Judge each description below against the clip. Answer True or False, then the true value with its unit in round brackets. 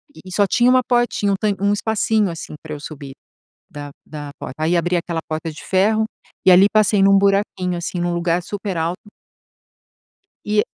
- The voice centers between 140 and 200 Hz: True (185 Hz)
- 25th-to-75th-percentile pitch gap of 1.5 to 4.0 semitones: True (3.7 semitones)